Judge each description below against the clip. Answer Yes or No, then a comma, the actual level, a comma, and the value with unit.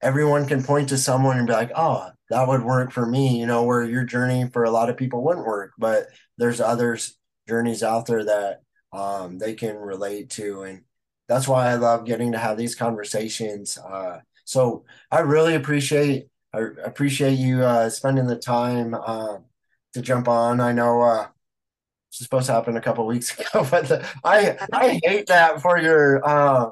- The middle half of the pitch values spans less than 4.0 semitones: Yes, narrow, 2.6 semitones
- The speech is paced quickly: No, average, 190 wpm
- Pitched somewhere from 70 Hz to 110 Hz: No, low, 120 Hz